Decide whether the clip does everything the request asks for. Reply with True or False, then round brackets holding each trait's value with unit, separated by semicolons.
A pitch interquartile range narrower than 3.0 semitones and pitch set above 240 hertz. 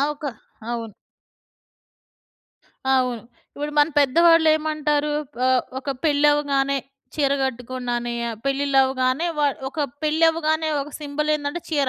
True (2.6 semitones; 285 Hz)